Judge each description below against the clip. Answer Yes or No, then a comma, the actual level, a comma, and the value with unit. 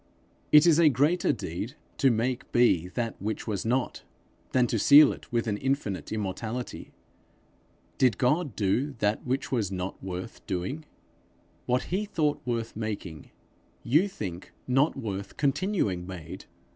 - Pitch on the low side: Yes, low, 115 Hz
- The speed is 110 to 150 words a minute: Yes, average, 145 wpm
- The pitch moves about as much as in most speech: No, wide, 5.8 semitones